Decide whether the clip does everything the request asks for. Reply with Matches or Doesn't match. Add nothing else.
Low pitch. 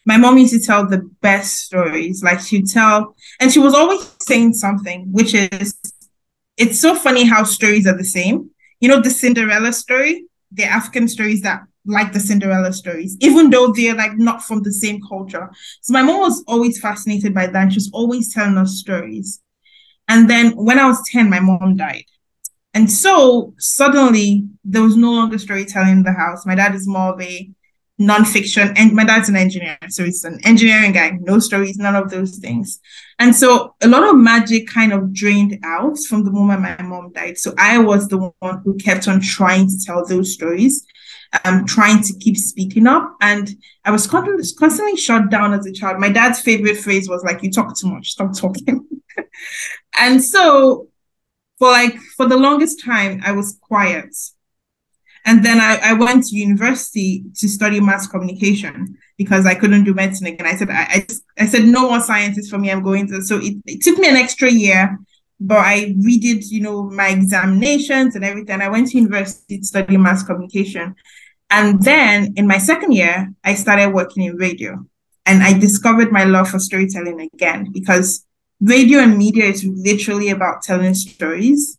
Doesn't match